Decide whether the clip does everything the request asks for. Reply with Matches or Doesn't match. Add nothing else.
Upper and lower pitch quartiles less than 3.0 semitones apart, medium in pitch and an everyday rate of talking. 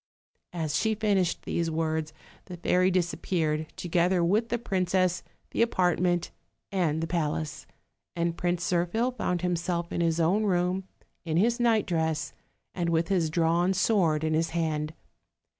Matches